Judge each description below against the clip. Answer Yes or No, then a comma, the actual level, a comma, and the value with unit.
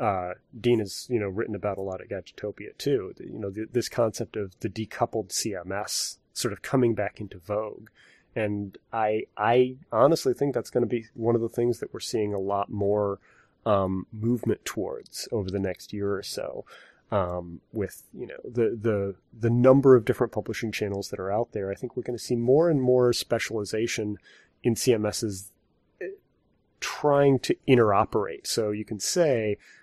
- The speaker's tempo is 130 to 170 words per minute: No, average, 180 wpm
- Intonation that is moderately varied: Yes, average, 3.0 semitones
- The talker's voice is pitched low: Yes, low, 110 Hz